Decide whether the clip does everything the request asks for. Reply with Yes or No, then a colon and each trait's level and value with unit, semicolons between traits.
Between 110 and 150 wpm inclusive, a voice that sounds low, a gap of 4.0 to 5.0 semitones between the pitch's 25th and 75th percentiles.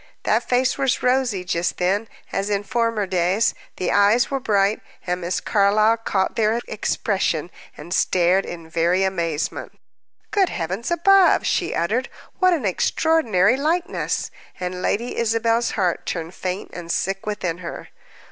No: average, 145 wpm; high, 200 Hz; average, 4.7 semitones